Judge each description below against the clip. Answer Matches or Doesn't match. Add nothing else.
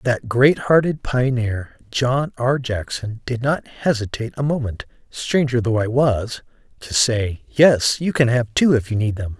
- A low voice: Matches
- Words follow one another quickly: Doesn't match